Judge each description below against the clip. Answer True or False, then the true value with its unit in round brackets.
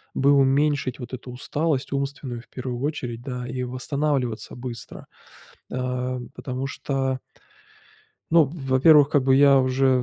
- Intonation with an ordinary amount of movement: False (1.8 semitones)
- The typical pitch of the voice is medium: False (130 Hz)